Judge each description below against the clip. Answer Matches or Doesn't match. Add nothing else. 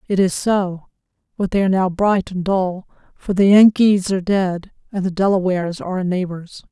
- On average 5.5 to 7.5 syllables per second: Doesn't match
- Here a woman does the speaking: Matches